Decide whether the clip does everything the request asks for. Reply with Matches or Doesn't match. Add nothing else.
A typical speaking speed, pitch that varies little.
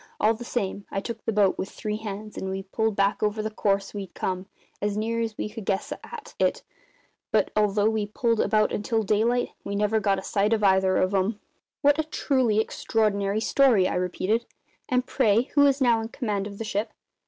Doesn't match